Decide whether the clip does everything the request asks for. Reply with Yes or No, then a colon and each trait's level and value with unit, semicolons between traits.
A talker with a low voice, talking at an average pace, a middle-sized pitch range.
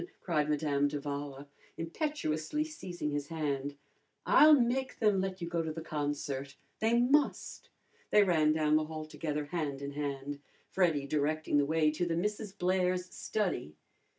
No: medium, 155 Hz; average, 150 wpm; average, 4.4 semitones